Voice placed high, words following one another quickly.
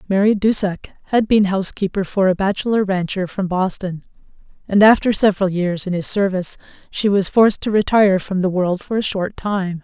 No: high, 195 Hz; average, 185 wpm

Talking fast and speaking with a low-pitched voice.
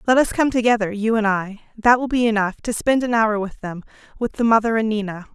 No: fast, 245 wpm; high, 220 Hz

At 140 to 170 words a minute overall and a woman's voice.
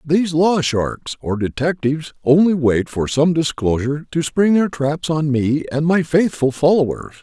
No: average, 165 wpm; male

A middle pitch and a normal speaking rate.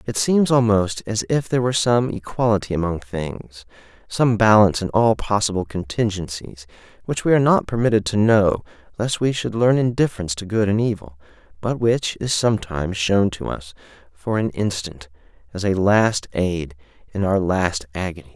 No: low, 100 Hz; average, 165 wpm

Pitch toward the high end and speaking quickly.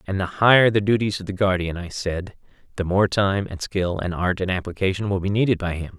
No: very low, 95 Hz; fast, 240 wpm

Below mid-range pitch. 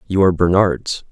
Yes: very low, 90 Hz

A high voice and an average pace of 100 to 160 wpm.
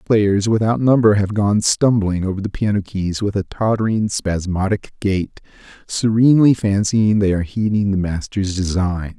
No: low, 100 Hz; average, 150 wpm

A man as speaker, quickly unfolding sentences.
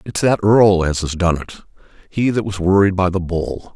Yes: male; fast, 210 wpm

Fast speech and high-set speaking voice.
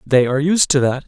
No: fast, 280 wpm; medium, 145 Hz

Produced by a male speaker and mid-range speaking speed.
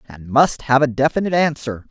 Yes: male; average, 190 wpm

